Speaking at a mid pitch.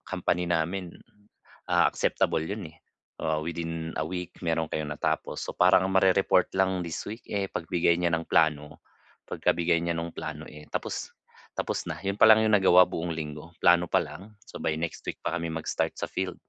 No: very low, 85 Hz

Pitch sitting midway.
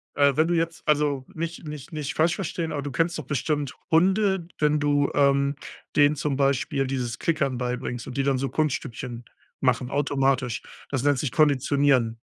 Yes: medium, 145 Hz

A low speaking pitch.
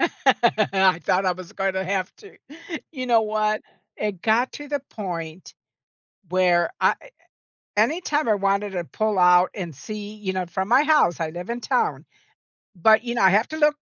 No: high, 205 Hz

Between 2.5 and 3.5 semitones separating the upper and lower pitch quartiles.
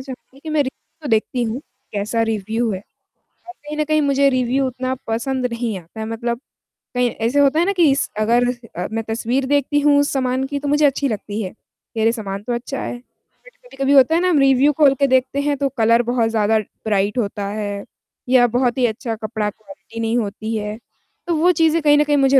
No: average, 4.1 semitones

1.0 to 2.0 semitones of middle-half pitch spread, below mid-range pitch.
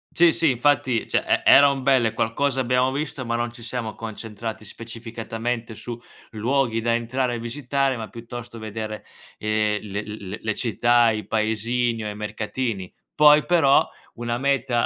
No: average, 2.7 semitones; low, 115 Hz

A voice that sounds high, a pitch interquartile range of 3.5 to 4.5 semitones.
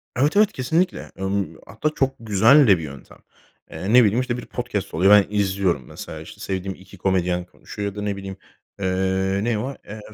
No: low, 100 Hz; average, 4.2 semitones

